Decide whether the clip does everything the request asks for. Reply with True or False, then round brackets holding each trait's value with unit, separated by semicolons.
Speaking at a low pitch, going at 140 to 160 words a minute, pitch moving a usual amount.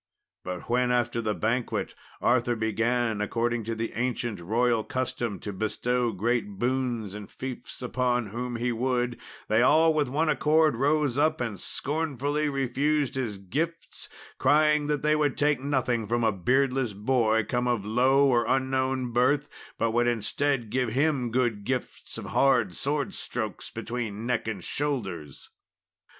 True (125 Hz; 150 wpm; 3.2 semitones)